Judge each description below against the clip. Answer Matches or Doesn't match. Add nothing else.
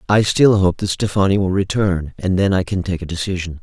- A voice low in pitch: Matches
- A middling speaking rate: Doesn't match